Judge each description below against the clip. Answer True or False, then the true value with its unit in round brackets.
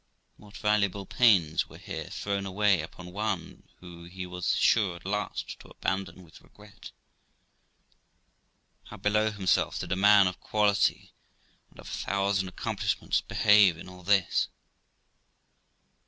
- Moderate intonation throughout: False (2.2 semitones)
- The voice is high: False (100 Hz)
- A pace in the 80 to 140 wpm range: True (135 wpm)